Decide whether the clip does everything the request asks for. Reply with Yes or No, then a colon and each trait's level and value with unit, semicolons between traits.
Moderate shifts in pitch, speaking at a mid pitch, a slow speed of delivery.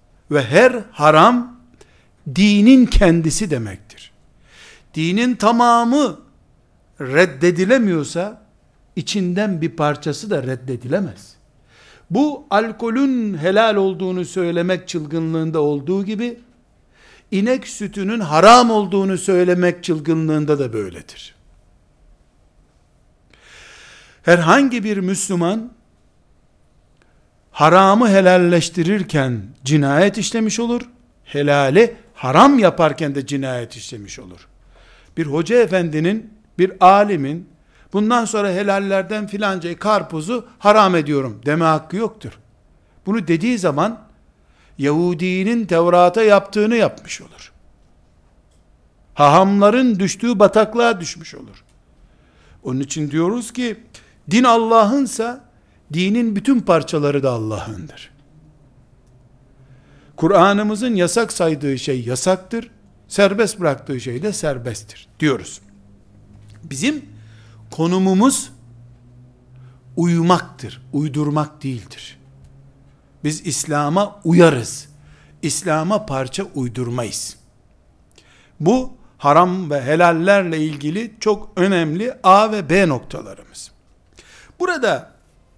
No: wide, 7.7 semitones; medium, 170 Hz; slow, 85 wpm